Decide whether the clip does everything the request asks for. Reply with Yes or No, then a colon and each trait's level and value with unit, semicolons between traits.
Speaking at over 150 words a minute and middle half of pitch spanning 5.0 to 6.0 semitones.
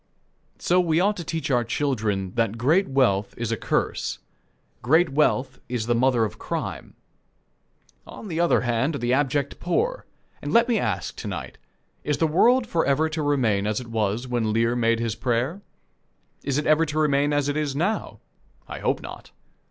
Yes: average, 185 wpm; wide, 5.4 semitones